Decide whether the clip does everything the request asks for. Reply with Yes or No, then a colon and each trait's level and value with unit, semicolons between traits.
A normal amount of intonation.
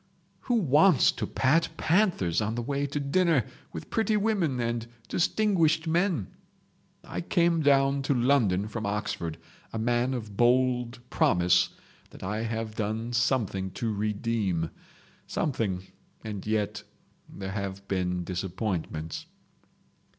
No: wide, 6.2 semitones